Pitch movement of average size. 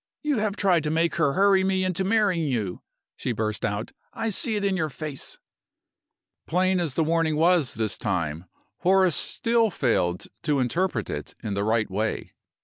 No: wide, 8.9 semitones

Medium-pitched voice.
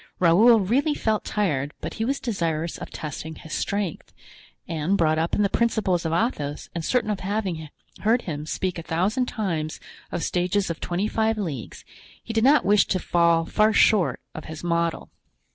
Yes: medium, 180 Hz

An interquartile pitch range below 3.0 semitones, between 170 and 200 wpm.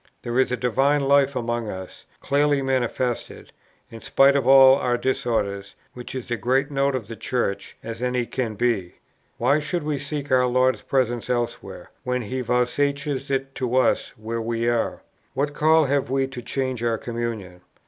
Yes: narrow, 2.6 semitones; average, 180 wpm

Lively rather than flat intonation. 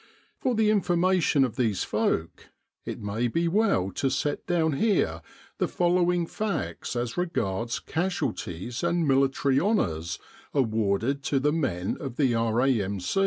Yes: wide, 7.6 semitones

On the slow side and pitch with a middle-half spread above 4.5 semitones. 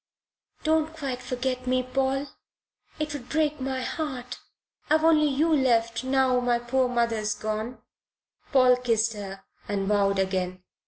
No: slow, 130 wpm; average, 3.3 semitones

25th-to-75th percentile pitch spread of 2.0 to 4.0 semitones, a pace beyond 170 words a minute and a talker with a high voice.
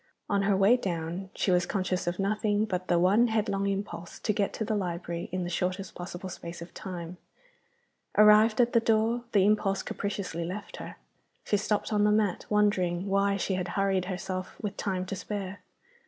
Yes: narrow, 2.4 semitones; average, 185 wpm; high, 195 Hz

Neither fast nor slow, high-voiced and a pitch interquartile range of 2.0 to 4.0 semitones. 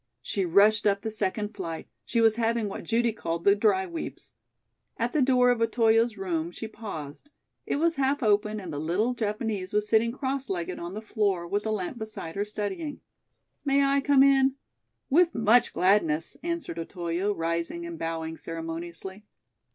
No: average, 175 wpm; high, 210 Hz; average, 5.1 semitones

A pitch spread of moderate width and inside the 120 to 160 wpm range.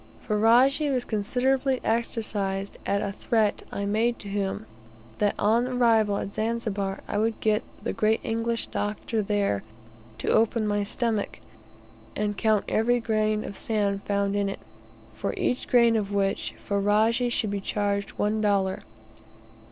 No: narrow, 2.2 semitones; average, 145 wpm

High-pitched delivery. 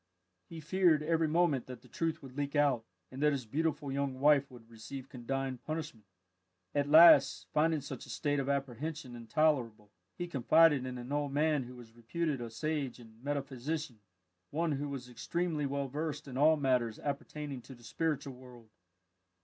No: medium, 140 Hz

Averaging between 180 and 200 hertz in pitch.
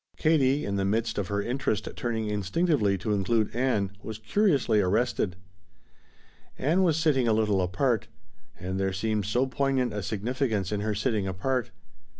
No: low, 110 Hz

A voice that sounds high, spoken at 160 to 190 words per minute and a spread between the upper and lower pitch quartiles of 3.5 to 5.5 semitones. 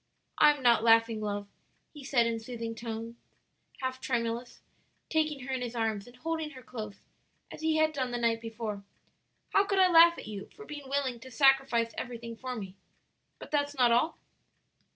Yes: high, 245 Hz; average, 185 wpm; average, 3.9 semitones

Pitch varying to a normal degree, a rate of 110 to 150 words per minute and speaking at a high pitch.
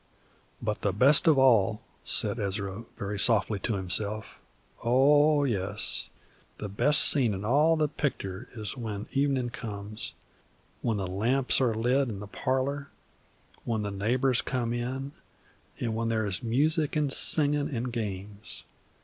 No: average, 4.7 semitones; average, 145 wpm; low, 115 Hz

